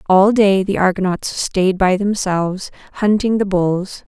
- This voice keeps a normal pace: Yes, average, 145 wpm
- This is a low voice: No, high, 190 Hz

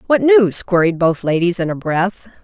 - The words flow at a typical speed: Yes, average, 195 wpm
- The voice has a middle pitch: Yes, medium, 180 Hz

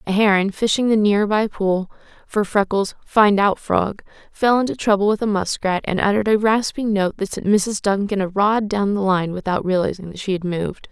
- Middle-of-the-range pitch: No, high, 200 Hz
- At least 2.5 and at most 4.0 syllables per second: No, 5.2 syllables/s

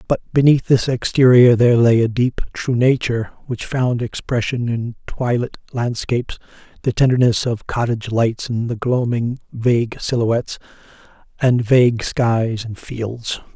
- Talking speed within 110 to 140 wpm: Yes, slow, 135 wpm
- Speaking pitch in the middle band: No, low, 120 Hz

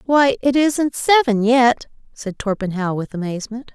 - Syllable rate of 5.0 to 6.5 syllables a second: No, 4.5 syllables/s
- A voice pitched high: Yes, high, 240 Hz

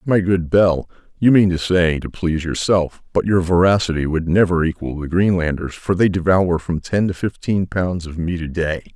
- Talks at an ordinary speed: No, fast, 210 wpm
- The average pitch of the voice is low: Yes, very low, 90 Hz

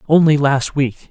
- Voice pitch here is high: No, medium, 145 Hz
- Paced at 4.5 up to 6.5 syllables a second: No, 4.1 syllables/s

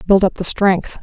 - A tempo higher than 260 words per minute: No, fast, 235 wpm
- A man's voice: No, female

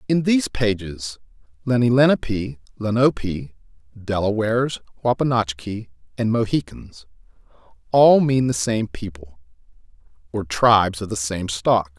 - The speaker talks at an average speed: No, slow, 105 wpm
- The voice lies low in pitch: Yes, low, 110 Hz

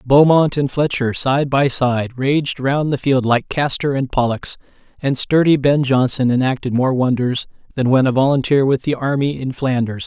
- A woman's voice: No, male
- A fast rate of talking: No, average, 180 wpm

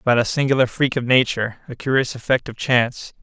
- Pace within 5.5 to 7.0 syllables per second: Yes, 6.3 syllables/s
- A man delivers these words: Yes, male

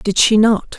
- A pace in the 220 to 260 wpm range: Yes, fast, 230 wpm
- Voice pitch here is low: No, high, 210 Hz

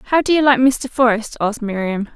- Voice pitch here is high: Yes, high, 240 Hz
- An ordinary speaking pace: No, fast, 225 wpm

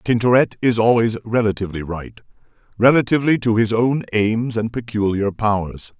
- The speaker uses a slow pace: Yes, slow, 120 wpm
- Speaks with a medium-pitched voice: No, low, 115 Hz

